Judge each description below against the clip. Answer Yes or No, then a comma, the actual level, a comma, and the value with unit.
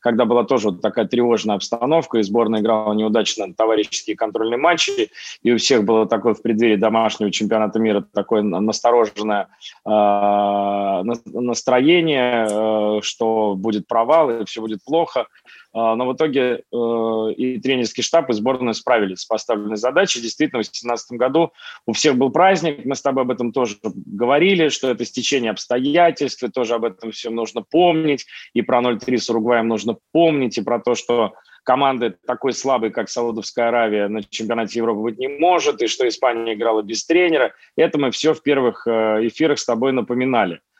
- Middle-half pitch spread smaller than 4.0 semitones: Yes, average, 3.0 semitones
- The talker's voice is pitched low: Yes, low, 120 Hz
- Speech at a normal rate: No, fast, 170 wpm